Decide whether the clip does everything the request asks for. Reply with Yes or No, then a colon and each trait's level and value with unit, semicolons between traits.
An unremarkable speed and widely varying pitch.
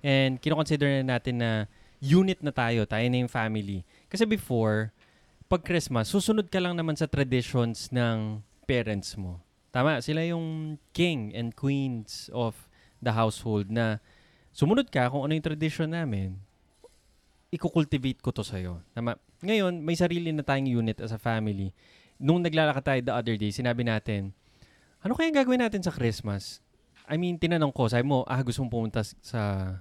No: fast, 165 wpm; wide, 6.1 semitones